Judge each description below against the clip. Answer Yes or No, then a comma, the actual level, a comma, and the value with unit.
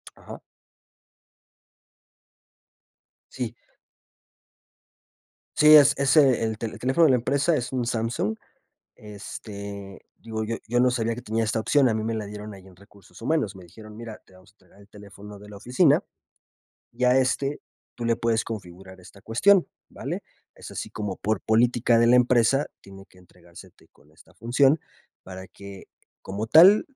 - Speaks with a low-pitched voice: Yes, low, 110 Hz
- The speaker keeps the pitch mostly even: No, average, 3.8 semitones